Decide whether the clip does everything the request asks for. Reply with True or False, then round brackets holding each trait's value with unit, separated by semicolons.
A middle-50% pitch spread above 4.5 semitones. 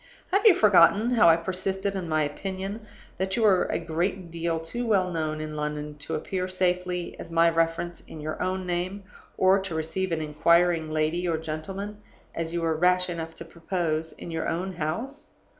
False (2.8 semitones)